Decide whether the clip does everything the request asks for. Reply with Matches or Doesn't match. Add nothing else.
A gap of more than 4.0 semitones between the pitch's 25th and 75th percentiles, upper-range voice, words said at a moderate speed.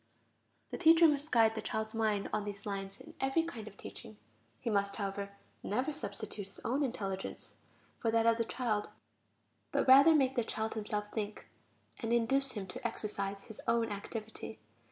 Doesn't match